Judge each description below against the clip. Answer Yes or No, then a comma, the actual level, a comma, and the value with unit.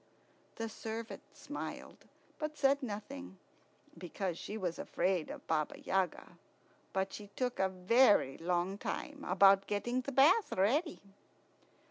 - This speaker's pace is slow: Yes, slow, 125 wpm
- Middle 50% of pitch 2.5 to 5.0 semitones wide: No, wide, 5.6 semitones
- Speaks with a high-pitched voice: Yes, high, 205 Hz